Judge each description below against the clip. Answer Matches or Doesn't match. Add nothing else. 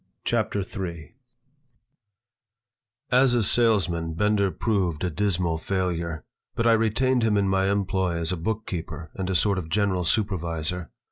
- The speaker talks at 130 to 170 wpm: Matches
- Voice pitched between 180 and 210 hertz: Doesn't match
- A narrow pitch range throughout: Doesn't match